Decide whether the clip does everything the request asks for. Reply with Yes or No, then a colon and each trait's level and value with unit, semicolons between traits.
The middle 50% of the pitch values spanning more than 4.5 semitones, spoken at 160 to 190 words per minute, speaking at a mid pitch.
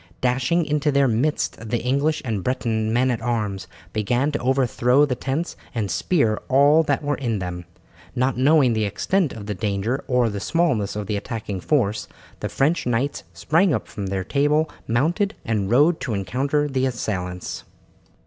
No: average, 5.1 semitones; average, 170 wpm; low, 125 Hz